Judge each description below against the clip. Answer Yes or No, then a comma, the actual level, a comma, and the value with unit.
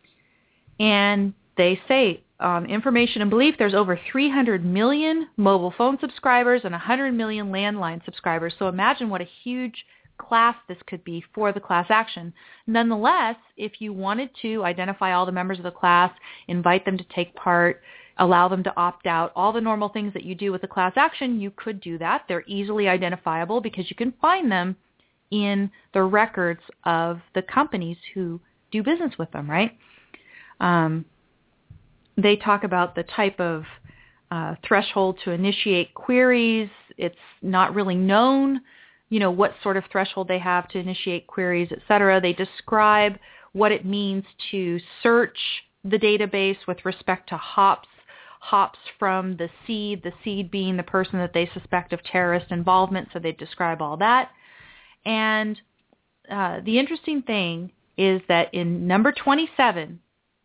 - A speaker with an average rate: Yes, average, 160 wpm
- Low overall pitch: No, high, 195 Hz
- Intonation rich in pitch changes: No, average, 3.6 semitones